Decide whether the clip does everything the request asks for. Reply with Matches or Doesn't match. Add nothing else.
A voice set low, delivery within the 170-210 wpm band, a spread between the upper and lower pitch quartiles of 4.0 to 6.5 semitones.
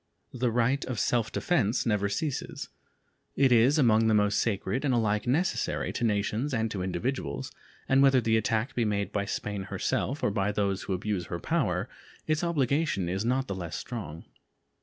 Matches